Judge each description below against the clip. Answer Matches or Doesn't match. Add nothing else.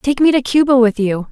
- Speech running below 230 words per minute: Doesn't match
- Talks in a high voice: Matches